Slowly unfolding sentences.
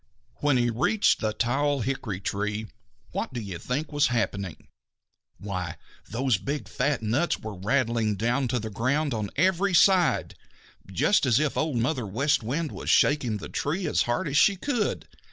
No: average, 170 wpm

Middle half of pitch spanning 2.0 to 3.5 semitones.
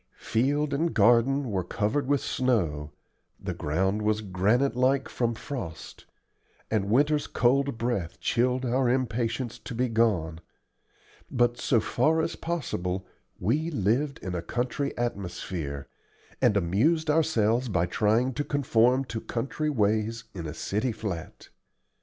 No: average, 5.1 semitones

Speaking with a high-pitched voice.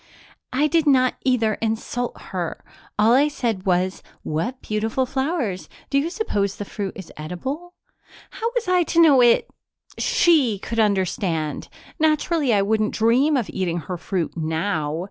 Yes: high, 225 Hz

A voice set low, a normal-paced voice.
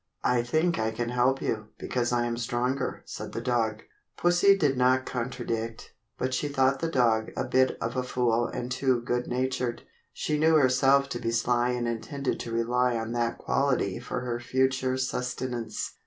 Yes: low, 125 Hz; average, 185 wpm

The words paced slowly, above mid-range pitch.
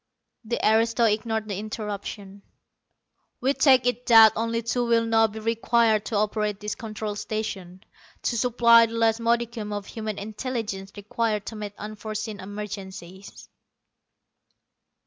Yes: slow, 130 wpm; high, 220 Hz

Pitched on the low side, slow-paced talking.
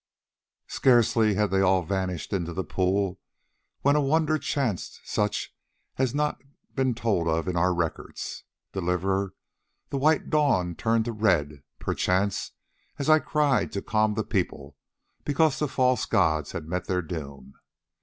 No: low, 100 Hz; average, 150 wpm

